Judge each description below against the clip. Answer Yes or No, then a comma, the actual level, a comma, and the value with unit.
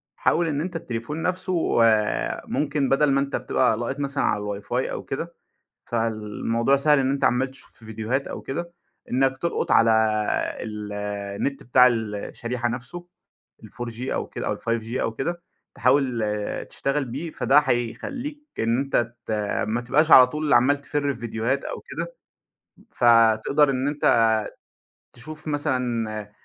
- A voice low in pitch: Yes, low, 130 Hz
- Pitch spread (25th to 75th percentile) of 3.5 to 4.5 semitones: Yes, average, 4.1 semitones